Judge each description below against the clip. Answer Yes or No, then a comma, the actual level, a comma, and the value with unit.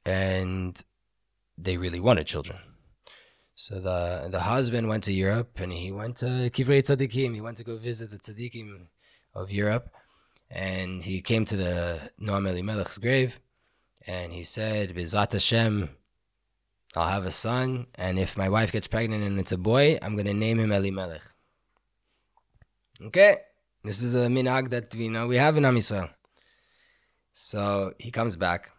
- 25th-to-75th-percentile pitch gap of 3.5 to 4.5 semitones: Yes, average, 4.0 semitones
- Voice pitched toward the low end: Yes, low, 105 Hz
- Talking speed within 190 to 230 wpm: No, average, 155 wpm